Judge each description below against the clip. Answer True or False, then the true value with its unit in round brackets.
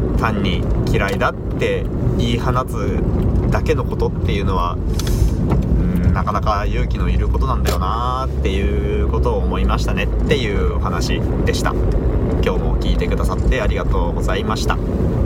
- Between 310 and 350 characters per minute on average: True (325 characters per minute)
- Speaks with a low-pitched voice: True (85 Hz)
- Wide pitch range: True (6.3 semitones)